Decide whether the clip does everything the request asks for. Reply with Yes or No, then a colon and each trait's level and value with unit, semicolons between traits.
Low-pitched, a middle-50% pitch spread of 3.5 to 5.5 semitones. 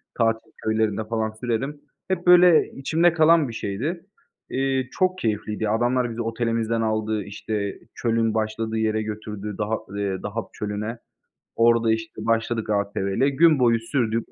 No: low, 115 Hz; average, 2.8 semitones